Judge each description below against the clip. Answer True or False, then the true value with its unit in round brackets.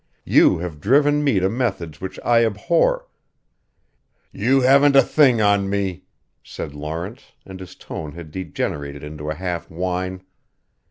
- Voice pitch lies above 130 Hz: False (95 Hz)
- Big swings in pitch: True (6.9 semitones)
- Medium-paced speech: True (150 wpm)